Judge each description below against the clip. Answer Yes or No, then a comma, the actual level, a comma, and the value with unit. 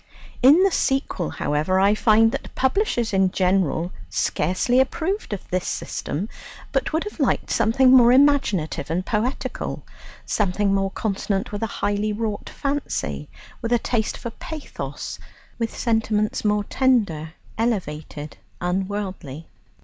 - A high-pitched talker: Yes, high, 210 Hz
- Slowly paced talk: Yes, slow, 130 wpm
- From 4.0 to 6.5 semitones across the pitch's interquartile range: Yes, average, 4.8 semitones